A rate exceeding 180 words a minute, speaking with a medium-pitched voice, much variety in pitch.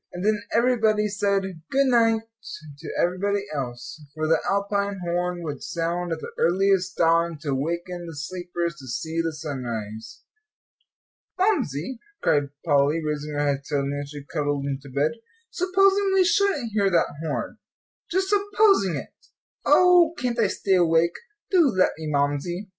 No: average, 150 wpm; medium, 175 Hz; wide, 6.7 semitones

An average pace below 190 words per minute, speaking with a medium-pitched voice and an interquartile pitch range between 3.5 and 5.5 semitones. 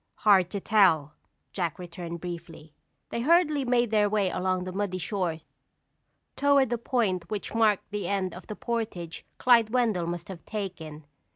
No: average, 160 wpm; high, 195 Hz; average, 4.5 semitones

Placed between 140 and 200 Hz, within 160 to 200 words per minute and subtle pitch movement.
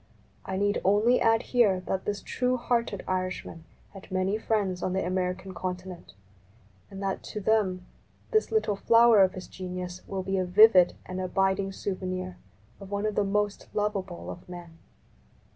Yes: high, 190 Hz; average, 165 wpm; narrow, 2.2 semitones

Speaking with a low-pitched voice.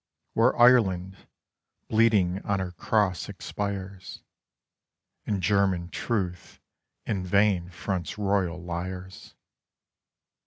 Yes: very low, 95 Hz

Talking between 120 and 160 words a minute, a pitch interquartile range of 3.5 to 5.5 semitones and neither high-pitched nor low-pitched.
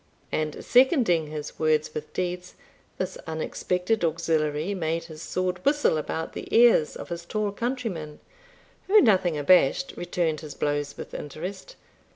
Yes: average, 140 wpm; average, 4.1 semitones; medium, 170 Hz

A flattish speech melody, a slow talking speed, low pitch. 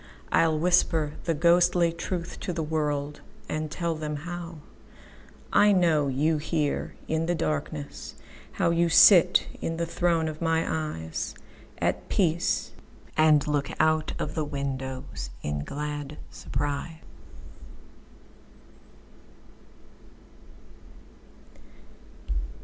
No: narrow, 2.3 semitones; slow, 90 wpm; medium, 155 Hz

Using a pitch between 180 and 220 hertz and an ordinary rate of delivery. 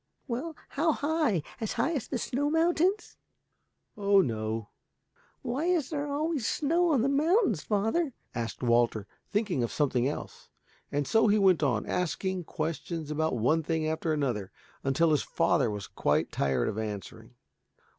Yes: medium, 185 Hz; average, 155 wpm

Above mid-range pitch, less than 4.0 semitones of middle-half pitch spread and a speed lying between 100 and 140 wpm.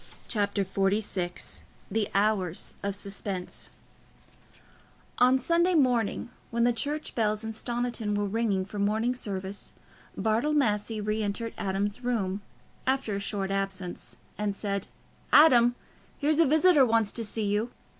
Yes: high, 215 Hz; average, 3.4 semitones; slow, 135 wpm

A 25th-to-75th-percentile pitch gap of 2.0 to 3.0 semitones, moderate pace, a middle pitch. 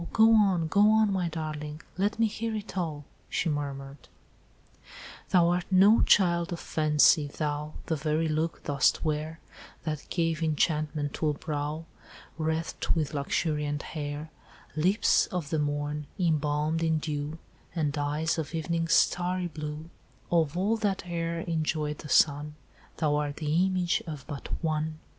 Yes: narrow, 2.4 semitones; average, 145 wpm; medium, 155 Hz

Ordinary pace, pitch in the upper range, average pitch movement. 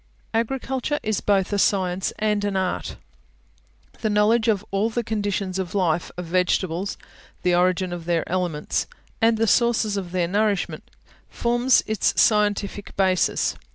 Yes: average, 150 wpm; high, 200 Hz; average, 3.1 semitones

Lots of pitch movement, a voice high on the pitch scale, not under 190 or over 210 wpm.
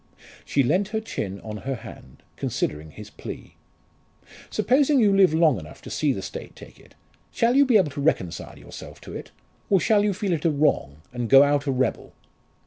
No: wide, 9.0 semitones; medium, 150 Hz; average, 200 wpm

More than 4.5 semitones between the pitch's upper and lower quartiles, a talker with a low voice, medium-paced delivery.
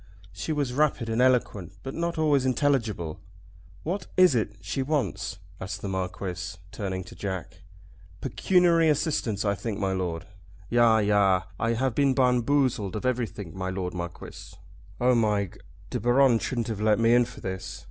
Yes: wide, 5.4 semitones; low, 115 Hz; average, 165 wpm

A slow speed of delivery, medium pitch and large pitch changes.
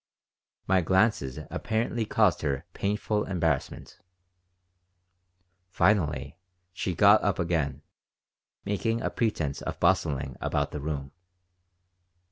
No: slow, 95 wpm; very low, 90 Hz; wide, 6.2 semitones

